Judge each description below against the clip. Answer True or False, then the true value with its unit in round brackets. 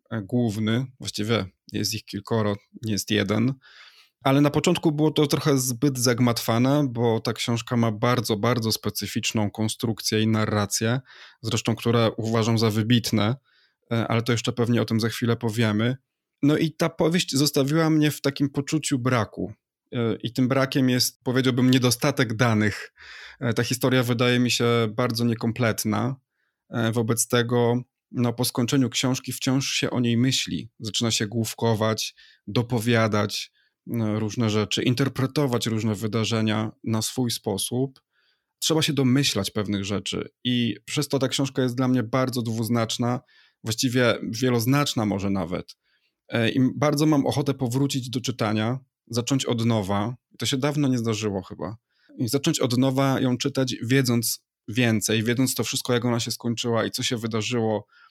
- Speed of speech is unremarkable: True (145 wpm)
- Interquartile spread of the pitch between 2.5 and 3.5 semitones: True (2.8 semitones)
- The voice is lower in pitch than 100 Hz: False (120 Hz)